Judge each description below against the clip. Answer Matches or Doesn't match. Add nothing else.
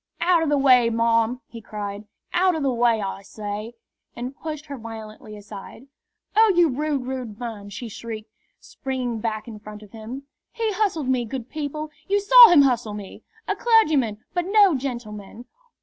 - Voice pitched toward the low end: Doesn't match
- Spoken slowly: Doesn't match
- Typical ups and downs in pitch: Doesn't match